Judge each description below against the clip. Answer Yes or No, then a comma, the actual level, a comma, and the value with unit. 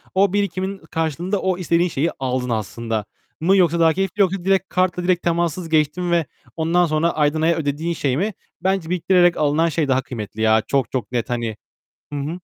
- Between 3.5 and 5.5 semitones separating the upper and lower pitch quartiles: Yes, average, 4.6 semitones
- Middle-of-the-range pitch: Yes, medium, 165 Hz